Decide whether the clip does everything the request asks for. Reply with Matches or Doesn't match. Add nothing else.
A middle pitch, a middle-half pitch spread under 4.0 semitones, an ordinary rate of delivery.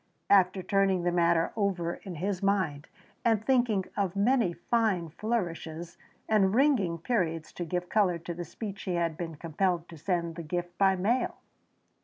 Matches